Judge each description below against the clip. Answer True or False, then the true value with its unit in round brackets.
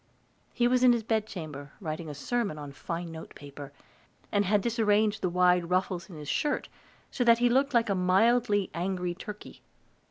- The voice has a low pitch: False (190 Hz)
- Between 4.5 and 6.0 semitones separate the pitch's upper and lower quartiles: True (5.3 semitones)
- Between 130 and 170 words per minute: False (180 wpm)